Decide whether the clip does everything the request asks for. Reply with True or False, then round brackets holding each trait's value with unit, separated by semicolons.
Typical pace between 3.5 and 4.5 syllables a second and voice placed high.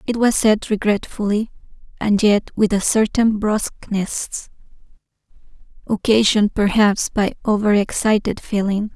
True (4.4 syllables/s; 210 Hz)